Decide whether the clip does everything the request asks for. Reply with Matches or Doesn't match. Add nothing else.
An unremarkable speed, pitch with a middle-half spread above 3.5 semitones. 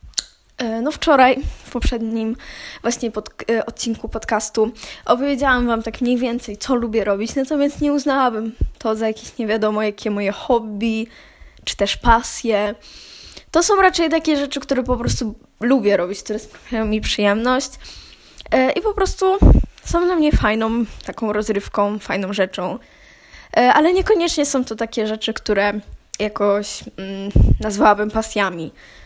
Matches